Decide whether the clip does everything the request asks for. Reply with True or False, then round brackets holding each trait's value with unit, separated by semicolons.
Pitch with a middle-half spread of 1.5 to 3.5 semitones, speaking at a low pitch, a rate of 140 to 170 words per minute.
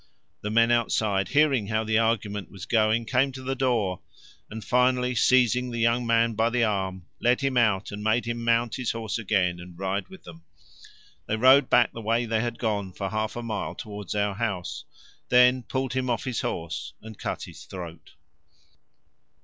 False (3.1 semitones; 115 Hz; 190 wpm)